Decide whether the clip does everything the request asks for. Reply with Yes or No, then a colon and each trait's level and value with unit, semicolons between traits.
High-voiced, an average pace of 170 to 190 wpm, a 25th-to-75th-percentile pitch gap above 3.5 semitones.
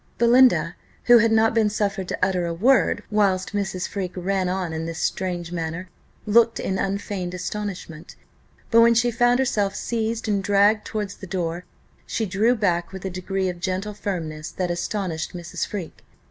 No: high, 195 Hz; average, 175 wpm; average, 3.2 semitones